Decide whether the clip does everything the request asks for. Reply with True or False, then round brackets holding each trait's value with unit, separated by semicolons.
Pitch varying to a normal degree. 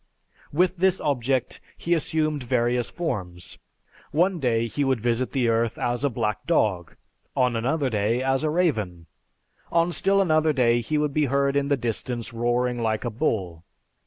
True (4.9 semitones)